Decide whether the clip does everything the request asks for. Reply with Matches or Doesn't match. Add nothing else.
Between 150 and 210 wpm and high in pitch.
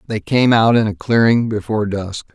Doesn't match